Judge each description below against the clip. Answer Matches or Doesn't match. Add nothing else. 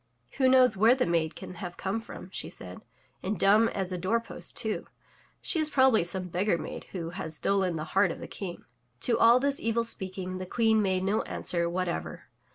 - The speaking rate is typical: Doesn't match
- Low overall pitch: Doesn't match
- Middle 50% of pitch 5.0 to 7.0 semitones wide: Doesn't match